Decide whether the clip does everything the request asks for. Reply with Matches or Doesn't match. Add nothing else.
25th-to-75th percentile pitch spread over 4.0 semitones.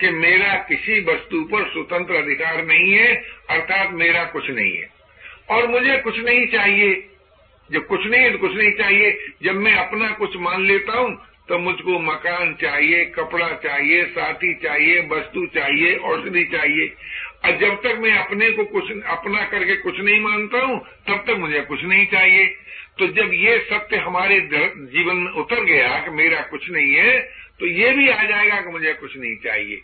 Matches